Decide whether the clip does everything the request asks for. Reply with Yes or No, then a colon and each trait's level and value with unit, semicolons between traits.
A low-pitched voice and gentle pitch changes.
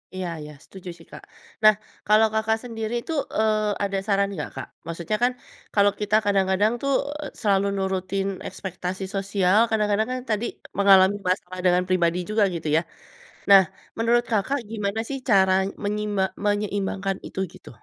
No: high, 200 Hz; narrow, 2.1 semitones